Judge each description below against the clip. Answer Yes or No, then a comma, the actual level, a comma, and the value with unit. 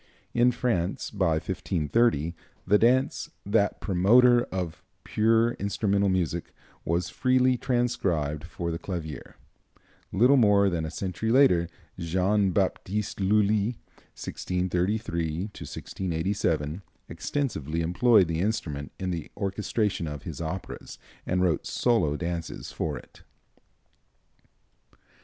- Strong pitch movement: No, average, 4.6 semitones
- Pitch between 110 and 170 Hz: No, very low, 95 Hz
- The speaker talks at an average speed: No, slow, 105 wpm